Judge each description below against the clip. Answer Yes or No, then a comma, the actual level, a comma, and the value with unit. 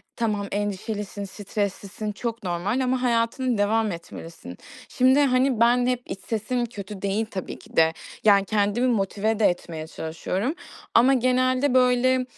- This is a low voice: No, high, 220 Hz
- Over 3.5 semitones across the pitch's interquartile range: Yes, average, 3.9 semitones